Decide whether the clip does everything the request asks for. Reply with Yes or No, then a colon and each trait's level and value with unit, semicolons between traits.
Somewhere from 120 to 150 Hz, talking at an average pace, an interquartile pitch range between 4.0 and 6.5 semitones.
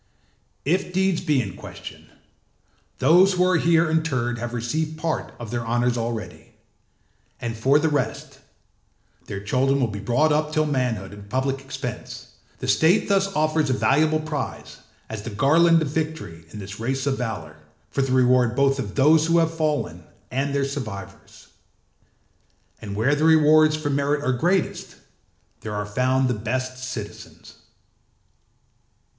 Yes: low, 135 Hz; average, 155 wpm; average, 4.7 semitones